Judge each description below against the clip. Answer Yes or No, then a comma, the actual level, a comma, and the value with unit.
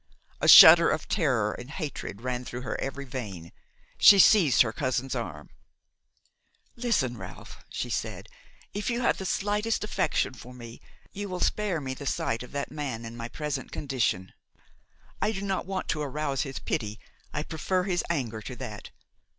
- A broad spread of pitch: Yes, wide, 6.9 semitones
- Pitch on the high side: No, low, 135 Hz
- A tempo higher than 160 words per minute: Yes, average, 170 wpm